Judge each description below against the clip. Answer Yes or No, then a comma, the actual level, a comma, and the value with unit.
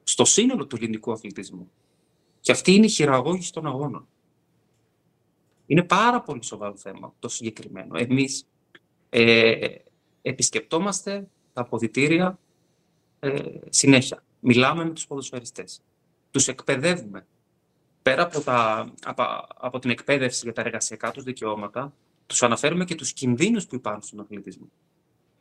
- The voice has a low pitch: Yes, low, 130 Hz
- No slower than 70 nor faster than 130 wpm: Yes, average, 125 wpm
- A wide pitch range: Yes, wide, 5.8 semitones